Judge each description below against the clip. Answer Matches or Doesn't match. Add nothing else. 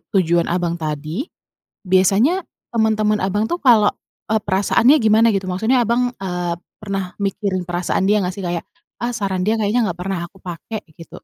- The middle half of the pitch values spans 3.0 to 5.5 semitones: Matches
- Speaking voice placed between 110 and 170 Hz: Doesn't match